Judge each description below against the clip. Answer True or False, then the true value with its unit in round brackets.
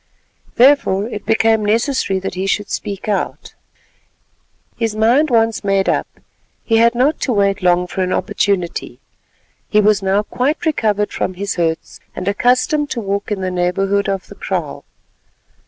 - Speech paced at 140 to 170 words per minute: True (155 wpm)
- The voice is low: False (205 Hz)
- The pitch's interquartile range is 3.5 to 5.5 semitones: False (3.1 semitones)